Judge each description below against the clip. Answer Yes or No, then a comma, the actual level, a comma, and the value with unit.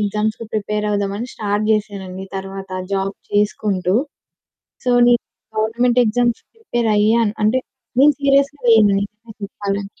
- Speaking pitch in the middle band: No, high, 210 Hz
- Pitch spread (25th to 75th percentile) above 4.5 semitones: No, narrow, 2.6 semitones